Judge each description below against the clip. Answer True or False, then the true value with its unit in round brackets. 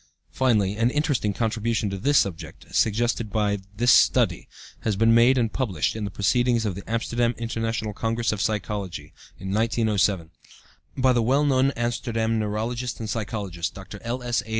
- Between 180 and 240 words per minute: False (155 wpm)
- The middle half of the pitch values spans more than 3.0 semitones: False (2.4 semitones)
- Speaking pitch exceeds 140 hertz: False (115 Hz)